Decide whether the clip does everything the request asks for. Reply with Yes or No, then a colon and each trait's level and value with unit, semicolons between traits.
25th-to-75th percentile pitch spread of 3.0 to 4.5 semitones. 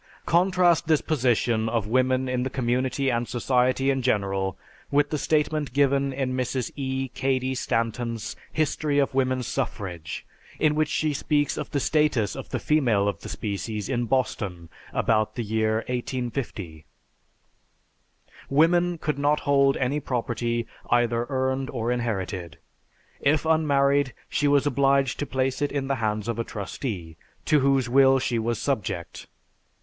Yes: average, 3.5 semitones